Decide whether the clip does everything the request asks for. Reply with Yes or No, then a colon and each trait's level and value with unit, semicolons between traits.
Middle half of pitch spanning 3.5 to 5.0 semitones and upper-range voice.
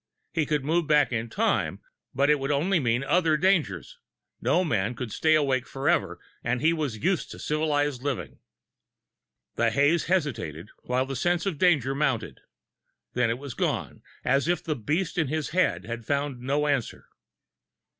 No: average, 4.2 semitones; medium, 145 Hz